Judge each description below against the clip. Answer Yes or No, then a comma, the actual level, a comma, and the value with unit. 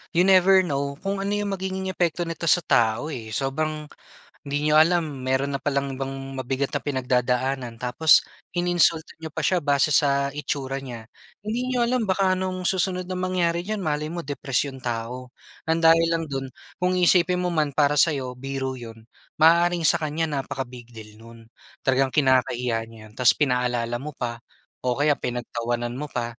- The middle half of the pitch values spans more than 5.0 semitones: Yes, wide, 5.4 semitones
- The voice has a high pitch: No, medium, 145 Hz